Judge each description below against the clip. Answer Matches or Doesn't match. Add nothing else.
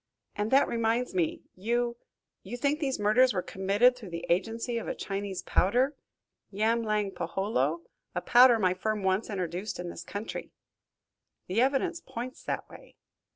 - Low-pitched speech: Doesn't match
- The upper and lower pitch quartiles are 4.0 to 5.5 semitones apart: Matches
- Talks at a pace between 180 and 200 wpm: Doesn't match